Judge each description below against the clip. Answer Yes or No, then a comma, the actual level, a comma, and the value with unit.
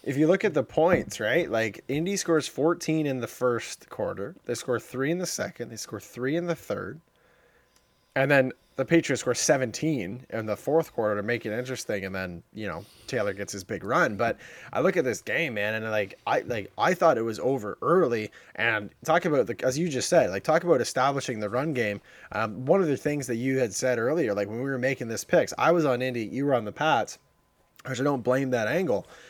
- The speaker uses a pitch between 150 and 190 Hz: No, low, 130 Hz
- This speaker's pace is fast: Yes, fast, 235 wpm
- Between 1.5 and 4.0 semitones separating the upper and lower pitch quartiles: No, average, 4.9 semitones